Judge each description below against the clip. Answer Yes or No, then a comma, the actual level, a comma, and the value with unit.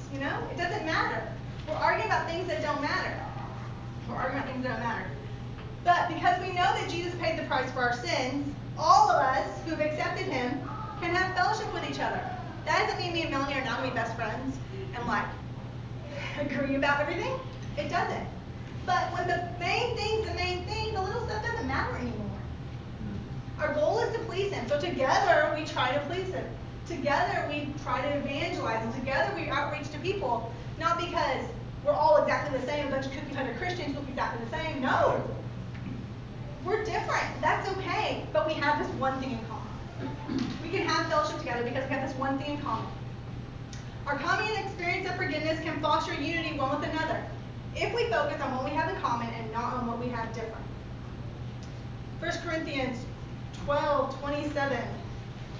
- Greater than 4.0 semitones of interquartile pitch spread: Yes, average, 4.7 semitones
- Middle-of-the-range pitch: No, very high, 305 Hz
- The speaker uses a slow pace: No, average, 190 wpm